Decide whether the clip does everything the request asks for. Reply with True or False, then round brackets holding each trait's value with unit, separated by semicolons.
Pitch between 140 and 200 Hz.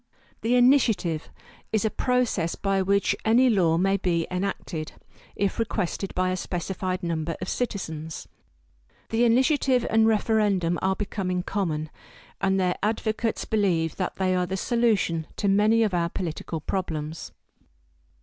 True (190 Hz)